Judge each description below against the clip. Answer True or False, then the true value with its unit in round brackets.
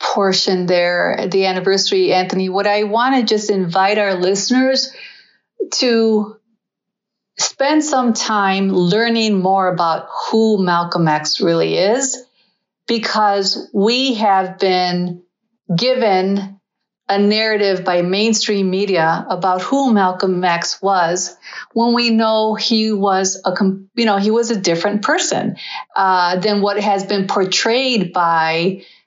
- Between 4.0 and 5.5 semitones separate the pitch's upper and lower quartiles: False (3.1 semitones)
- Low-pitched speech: False (200 Hz)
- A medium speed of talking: False (125 wpm)